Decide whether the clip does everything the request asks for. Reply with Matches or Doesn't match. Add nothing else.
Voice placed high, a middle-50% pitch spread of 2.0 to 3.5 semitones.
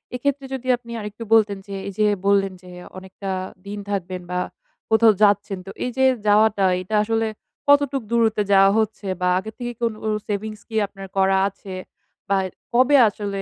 Matches